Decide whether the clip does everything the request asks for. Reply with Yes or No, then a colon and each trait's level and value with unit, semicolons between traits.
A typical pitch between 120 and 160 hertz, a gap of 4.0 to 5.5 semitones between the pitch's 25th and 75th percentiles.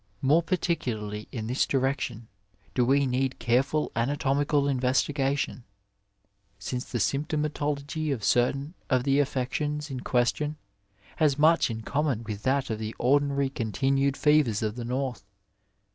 No: low, 135 Hz; average, 2.9 semitones